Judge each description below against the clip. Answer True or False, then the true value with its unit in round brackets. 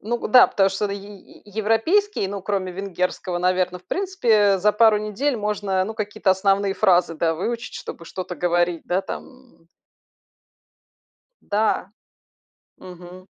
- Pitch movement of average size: True (3.0 semitones)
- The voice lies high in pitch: True (195 Hz)